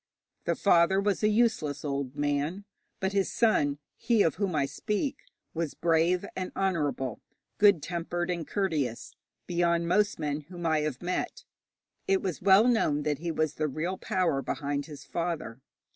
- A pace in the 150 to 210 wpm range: Yes, average, 160 wpm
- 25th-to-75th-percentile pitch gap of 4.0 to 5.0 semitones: Yes, average, 4.6 semitones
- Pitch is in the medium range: Yes, medium, 170 Hz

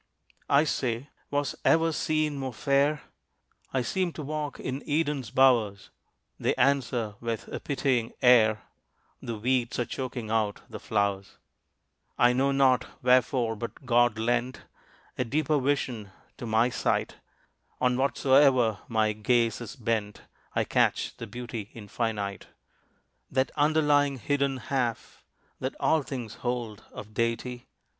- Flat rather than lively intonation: No, average, 3.5 semitones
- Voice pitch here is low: Yes, low, 125 Hz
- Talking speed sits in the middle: No, slow, 130 wpm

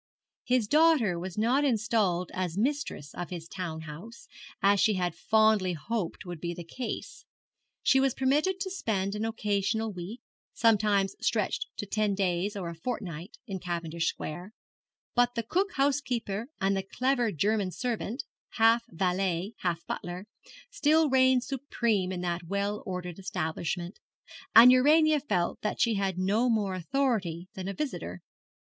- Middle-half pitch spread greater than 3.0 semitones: Yes, average, 5.2 semitones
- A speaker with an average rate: Yes, average, 150 wpm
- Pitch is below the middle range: No, high, 205 Hz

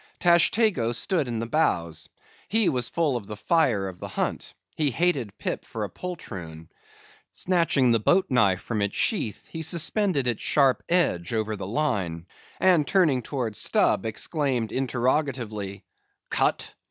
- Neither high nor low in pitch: No, low, 125 Hz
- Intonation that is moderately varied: No, wide, 7.5 semitones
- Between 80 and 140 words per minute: No, average, 150 wpm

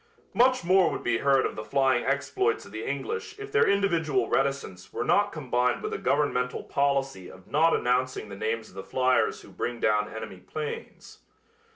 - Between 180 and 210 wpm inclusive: Yes, average, 185 wpm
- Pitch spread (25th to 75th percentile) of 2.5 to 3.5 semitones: No, average, 5.1 semitones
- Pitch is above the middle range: No, low, 135 Hz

